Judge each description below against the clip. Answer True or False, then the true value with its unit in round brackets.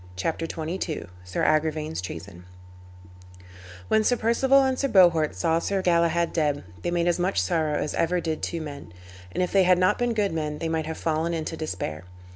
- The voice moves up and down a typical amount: True (3.0 semitones)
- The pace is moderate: True (190 wpm)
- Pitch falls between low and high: True (165 Hz)